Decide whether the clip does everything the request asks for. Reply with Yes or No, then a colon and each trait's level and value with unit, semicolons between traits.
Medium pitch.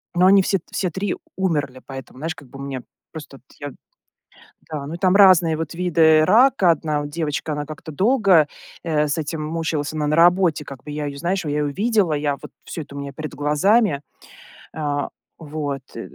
Yes: medium, 155 Hz